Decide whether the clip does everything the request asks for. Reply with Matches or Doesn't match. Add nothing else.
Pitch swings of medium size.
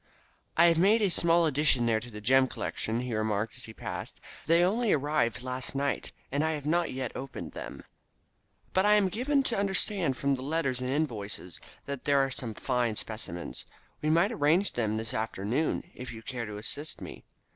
Doesn't match